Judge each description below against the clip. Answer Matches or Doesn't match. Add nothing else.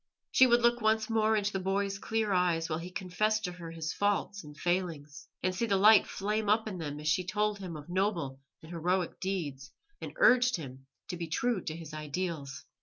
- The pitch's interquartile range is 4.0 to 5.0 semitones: Matches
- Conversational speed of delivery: Doesn't match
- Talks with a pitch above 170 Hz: Matches